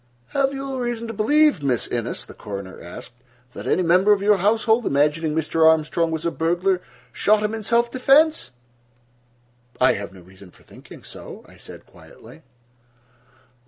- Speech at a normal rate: Yes, average, 160 wpm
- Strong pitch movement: Yes, wide, 7.4 semitones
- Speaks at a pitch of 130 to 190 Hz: Yes, medium, 185 Hz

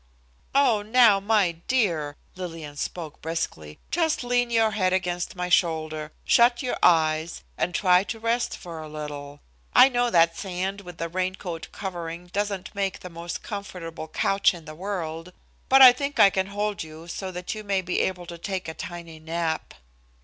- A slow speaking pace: No, average, 180 wpm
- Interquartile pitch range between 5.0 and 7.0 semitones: No, average, 3.7 semitones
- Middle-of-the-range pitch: Yes, medium, 180 Hz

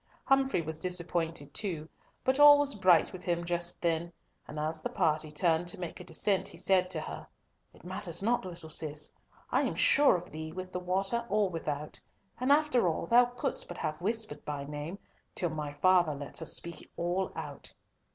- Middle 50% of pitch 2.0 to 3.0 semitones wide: No, average, 3.9 semitones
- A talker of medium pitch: Yes, medium, 175 Hz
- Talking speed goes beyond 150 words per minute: Yes, average, 190 wpm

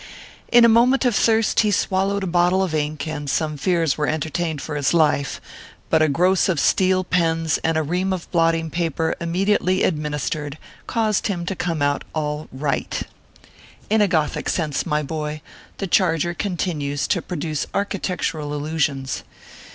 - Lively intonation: No, average, 3.7 semitones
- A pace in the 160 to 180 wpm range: Yes, average, 165 wpm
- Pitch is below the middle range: No, medium, 165 Hz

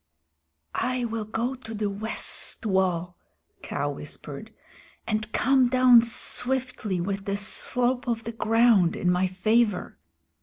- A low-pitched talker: No, high, 225 Hz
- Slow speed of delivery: Yes, slow, 125 wpm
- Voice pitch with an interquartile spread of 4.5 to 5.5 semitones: No, average, 3.7 semitones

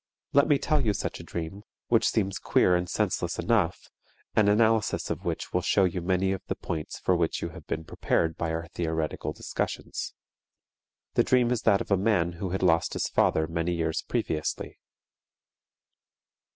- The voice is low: Yes, very low, 90 Hz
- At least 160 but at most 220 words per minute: Yes, average, 180 wpm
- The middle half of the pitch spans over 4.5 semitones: No, average, 4.1 semitones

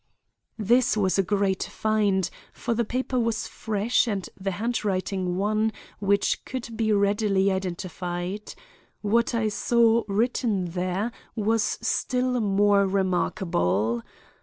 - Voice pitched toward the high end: Yes, high, 205 Hz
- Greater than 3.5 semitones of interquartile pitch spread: No, average, 3.0 semitones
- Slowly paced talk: Yes, slow, 115 wpm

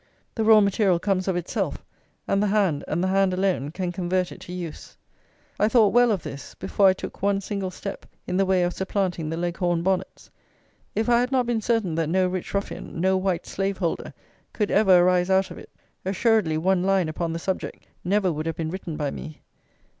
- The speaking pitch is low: No, medium, 185 Hz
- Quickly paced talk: Yes, fast, 210 wpm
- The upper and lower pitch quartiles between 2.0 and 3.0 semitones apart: Yes, narrow, 2.4 semitones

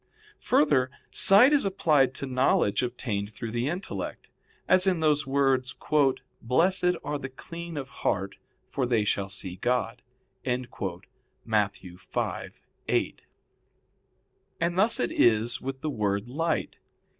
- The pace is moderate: No, slow, 120 wpm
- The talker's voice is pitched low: Yes, low, 130 Hz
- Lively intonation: Yes, wide, 6.1 semitones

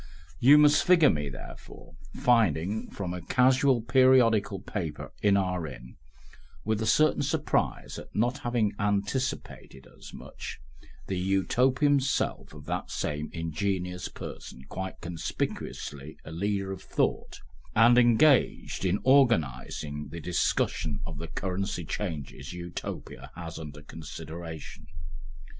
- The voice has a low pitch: Yes, very low, 95 Hz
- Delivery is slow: Yes, slow, 120 wpm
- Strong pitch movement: Yes, wide, 6.8 semitones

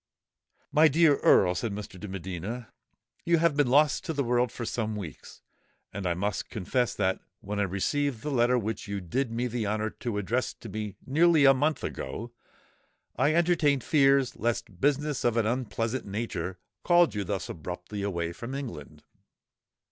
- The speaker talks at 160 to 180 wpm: Yes, average, 170 wpm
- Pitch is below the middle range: Yes, low, 115 Hz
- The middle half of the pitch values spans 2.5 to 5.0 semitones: No, wide, 5.6 semitones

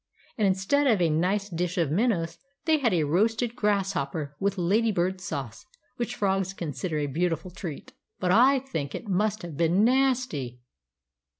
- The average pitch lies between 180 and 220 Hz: Yes, high, 190 Hz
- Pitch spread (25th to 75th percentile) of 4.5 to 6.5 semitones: Yes, average, 5.0 semitones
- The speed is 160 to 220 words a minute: Yes, average, 165 wpm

